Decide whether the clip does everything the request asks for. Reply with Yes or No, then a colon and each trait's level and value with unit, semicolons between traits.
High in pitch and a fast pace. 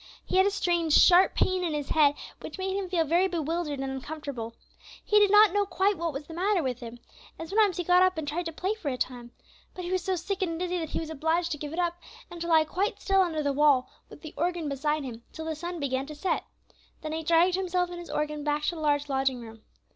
Yes: very high, 330 Hz; fast, 260 wpm